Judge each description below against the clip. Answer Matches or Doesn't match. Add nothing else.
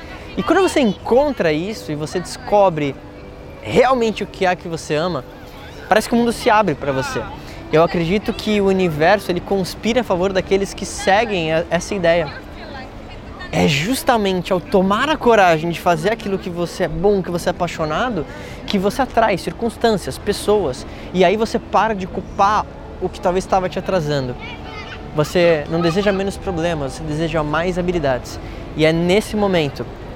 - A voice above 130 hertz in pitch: Matches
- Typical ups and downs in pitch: Matches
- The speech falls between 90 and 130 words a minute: Doesn't match